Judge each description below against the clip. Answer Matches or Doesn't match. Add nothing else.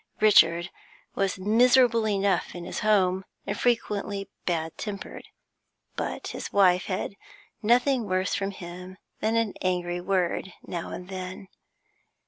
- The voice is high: Matches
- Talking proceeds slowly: Matches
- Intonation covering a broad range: Doesn't match